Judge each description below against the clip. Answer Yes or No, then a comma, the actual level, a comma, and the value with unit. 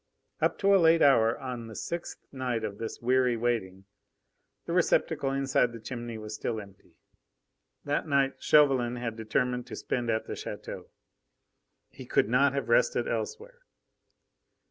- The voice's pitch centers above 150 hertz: No, low, 125 Hz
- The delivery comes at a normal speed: Yes, average, 150 wpm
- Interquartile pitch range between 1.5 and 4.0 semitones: Yes, average, 3.5 semitones